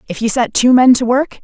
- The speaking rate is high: Yes, fast, 295 wpm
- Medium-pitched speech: No, high, 245 Hz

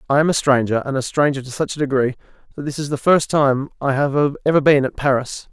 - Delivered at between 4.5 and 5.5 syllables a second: No, 5.9 syllables/s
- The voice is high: No, medium, 140 Hz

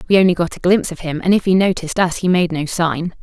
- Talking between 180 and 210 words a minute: No, fast, 295 wpm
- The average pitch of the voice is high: No, medium, 175 Hz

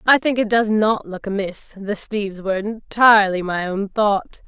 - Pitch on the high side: Yes, high, 205 Hz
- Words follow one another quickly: No, average, 190 wpm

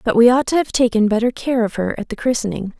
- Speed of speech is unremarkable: No, fast, 280 wpm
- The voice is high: Yes, high, 230 Hz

